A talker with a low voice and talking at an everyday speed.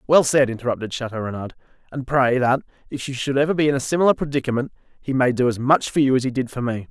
No: low, 130 Hz; fast, 250 wpm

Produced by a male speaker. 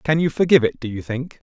Yes: male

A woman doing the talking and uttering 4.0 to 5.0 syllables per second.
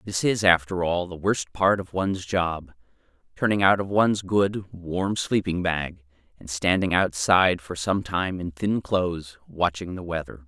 No: male; 4.4 syllables/s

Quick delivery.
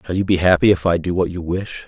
Yes: fast, 320 wpm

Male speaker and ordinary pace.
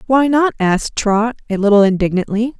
No: female; average, 160 wpm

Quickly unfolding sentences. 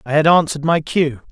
Yes: fast, 230 wpm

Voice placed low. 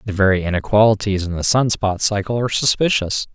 Yes: low, 105 Hz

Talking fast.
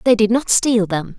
Yes: fast, 255 wpm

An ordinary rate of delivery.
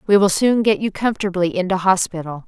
Yes: average, 195 wpm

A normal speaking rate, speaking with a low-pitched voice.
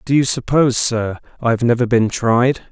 Yes: average, 175 wpm; low, 120 Hz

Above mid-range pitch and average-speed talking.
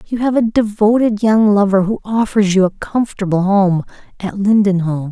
Yes: high, 205 Hz; average, 165 wpm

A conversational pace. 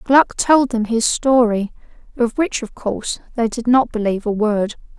Yes: average, 180 wpm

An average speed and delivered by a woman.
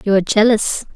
Yes: average, 190 wpm; female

